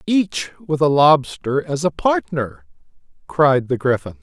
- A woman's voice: No, male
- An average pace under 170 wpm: Yes, average, 140 wpm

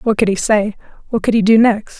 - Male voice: No, female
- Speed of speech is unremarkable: No, fast, 270 wpm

